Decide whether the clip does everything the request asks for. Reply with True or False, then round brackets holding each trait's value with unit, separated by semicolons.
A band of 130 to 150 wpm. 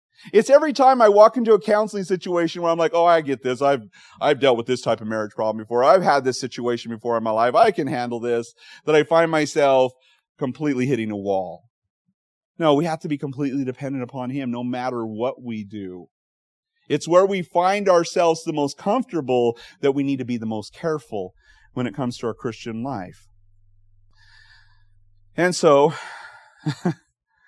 False (185 wpm)